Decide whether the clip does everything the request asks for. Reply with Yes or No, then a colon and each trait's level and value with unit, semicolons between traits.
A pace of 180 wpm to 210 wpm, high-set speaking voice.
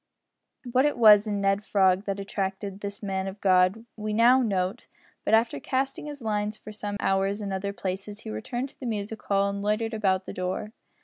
Yes: average, 200 wpm; high, 205 Hz